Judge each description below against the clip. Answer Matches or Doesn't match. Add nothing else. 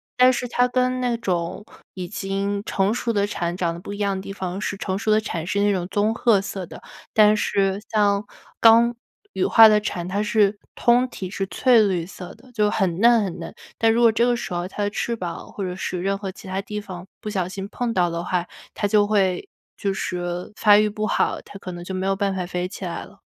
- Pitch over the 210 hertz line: Doesn't match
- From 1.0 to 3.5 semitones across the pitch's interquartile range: Matches